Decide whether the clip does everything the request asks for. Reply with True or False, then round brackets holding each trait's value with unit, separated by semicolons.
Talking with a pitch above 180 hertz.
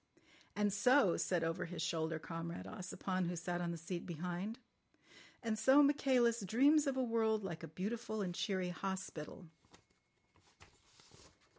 True (190 Hz)